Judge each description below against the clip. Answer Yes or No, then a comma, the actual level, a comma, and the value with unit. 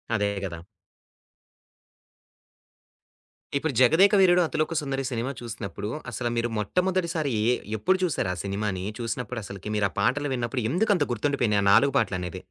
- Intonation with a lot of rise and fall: Yes, wide, 7.1 semitones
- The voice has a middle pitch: No, low, 125 Hz